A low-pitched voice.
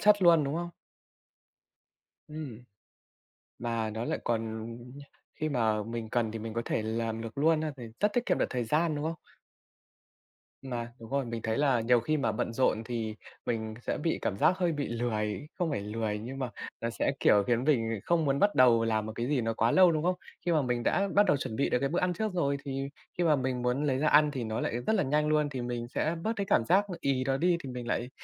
Yes: low, 130 Hz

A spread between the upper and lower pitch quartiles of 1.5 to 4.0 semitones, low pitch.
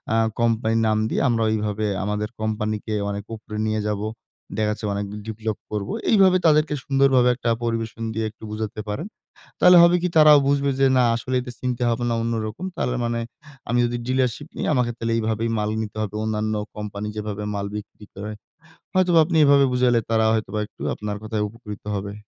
Yes: average, 3.0 semitones; low, 110 Hz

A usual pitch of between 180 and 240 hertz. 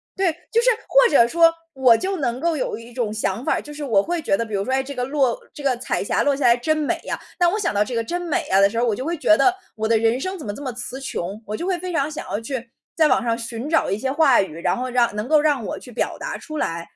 No: very high, 255 Hz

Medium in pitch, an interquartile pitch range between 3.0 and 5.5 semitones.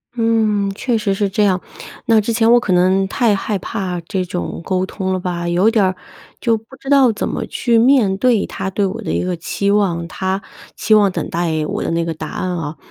No: high, 195 Hz; average, 3.6 semitones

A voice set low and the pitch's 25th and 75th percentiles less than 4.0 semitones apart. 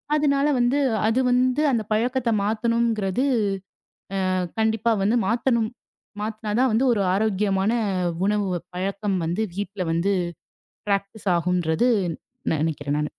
No: high, 215 Hz; average, 3.4 semitones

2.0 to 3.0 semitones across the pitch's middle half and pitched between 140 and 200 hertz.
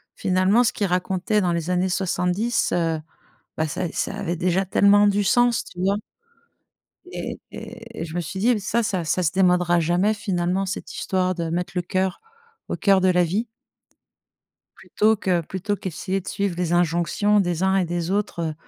Yes: narrow, 2.4 semitones; medium, 185 Hz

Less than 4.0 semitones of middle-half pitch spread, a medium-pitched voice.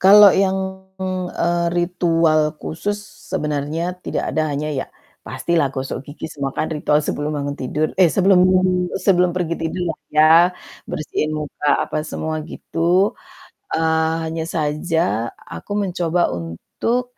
Yes: average, 2.8 semitones; medium, 160 Hz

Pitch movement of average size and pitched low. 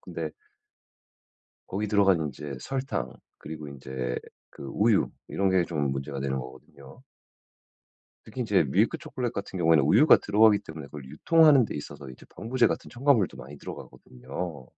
No: wide, 7.9 semitones; very low, 85 Hz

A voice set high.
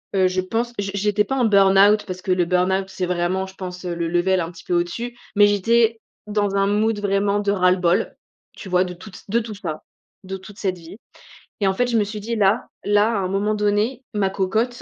Yes: high, 195 Hz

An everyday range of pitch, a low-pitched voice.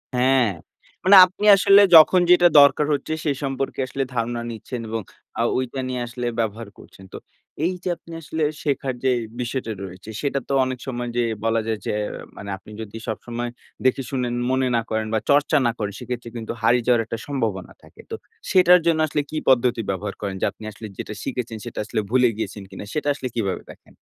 Yes: average, 3.7 semitones; low, 125 Hz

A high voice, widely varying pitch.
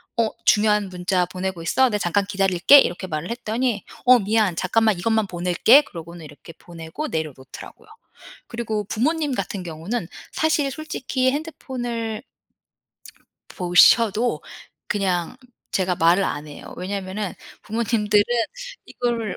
No: high, 205 Hz; average, 5.0 semitones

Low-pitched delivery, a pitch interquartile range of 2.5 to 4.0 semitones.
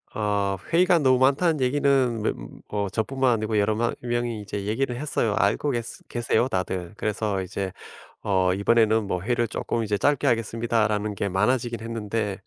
Yes: low, 115 Hz; average, 3.2 semitones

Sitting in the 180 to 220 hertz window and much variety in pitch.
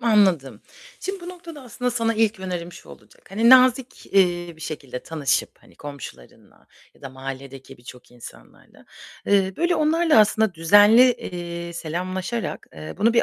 Yes: high, 190 Hz; wide, 7.0 semitones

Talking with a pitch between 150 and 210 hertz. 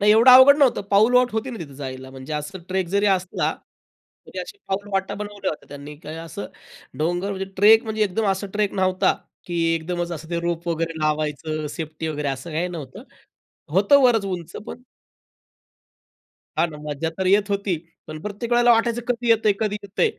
Yes: medium, 185 Hz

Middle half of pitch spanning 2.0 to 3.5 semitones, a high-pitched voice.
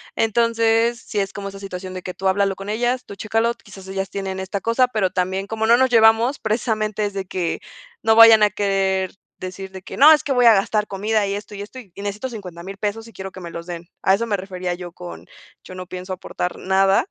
Yes: average, 2.9 semitones; high, 200 Hz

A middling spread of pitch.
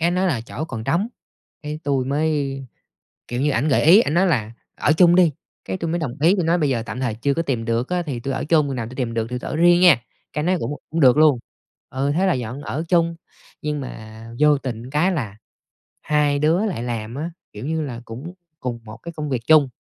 Yes: average, 4.9 semitones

